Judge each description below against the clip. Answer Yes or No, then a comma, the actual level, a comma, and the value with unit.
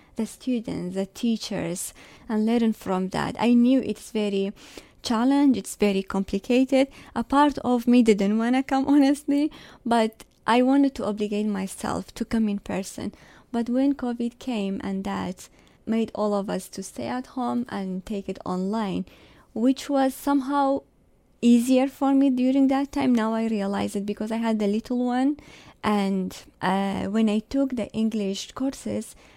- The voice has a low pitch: No, high, 225 Hz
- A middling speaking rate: Yes, average, 165 wpm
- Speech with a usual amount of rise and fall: Yes, average, 4.3 semitones